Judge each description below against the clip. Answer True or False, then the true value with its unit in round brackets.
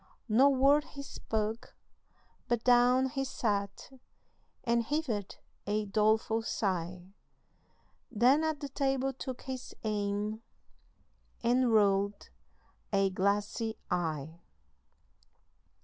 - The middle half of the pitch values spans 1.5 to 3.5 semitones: False (4.3 semitones)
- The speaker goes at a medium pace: False (95 wpm)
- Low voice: False (225 Hz)